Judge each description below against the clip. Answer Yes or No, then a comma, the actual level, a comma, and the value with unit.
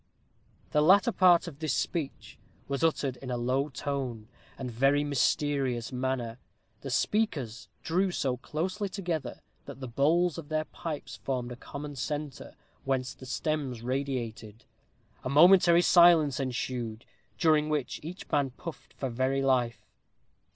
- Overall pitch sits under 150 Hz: Yes, medium, 140 Hz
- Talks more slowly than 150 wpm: Yes, average, 140 wpm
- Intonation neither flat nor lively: Yes, average, 3.8 semitones